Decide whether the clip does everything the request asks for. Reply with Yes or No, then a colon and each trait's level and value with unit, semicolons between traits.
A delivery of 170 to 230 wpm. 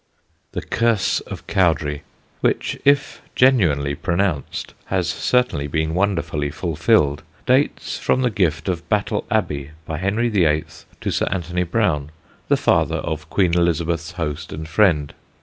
No: slow, 135 wpm